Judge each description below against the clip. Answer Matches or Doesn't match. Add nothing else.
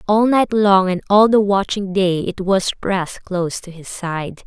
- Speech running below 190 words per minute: Doesn't match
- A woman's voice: Matches